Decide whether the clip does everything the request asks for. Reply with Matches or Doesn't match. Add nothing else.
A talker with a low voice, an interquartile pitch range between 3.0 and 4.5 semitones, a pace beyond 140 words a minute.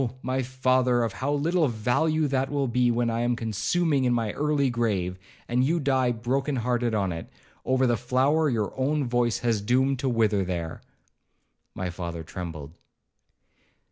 Matches